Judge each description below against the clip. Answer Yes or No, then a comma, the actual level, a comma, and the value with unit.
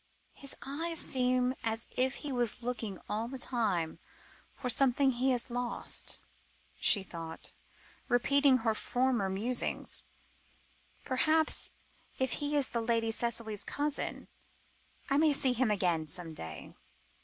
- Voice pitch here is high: Yes, high, 245 Hz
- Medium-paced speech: No, slow, 125 wpm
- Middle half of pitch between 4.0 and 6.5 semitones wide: No, average, 3.4 semitones